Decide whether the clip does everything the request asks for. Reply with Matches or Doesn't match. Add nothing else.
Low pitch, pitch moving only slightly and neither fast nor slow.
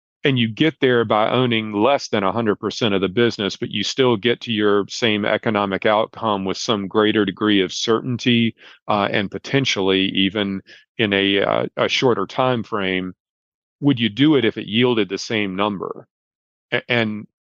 Doesn't match